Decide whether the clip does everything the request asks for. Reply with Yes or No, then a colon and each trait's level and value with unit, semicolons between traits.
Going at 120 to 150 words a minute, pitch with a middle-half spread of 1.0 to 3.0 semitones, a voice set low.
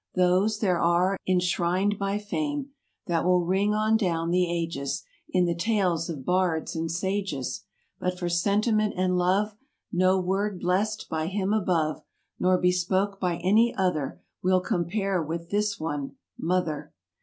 No: average, 140 wpm; average, 2.7 semitones; medium, 185 Hz